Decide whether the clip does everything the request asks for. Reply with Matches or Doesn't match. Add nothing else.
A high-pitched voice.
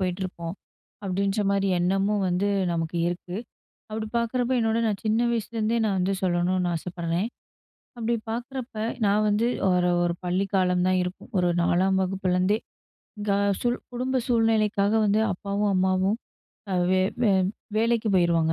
Matches